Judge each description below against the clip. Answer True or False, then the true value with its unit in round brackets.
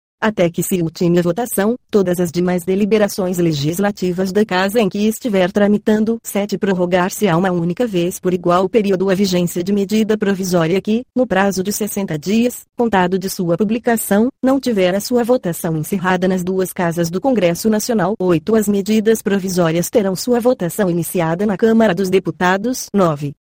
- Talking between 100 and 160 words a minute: False (170 wpm)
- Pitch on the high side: True (195 Hz)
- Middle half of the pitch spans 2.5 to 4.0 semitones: True (3.4 semitones)